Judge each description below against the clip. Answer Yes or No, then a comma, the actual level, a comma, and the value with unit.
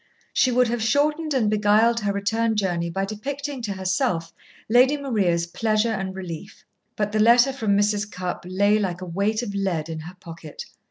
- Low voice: No, high, 210 Hz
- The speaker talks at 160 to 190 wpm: Yes, average, 180 wpm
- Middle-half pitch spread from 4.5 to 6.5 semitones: No, average, 3.8 semitones